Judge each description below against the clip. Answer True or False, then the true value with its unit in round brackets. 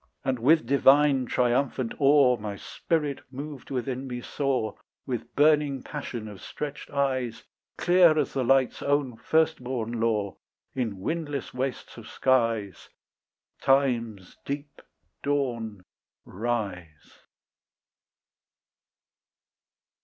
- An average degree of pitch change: True (3.6 semitones)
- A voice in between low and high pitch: False (130 Hz)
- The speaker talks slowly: True (100 wpm)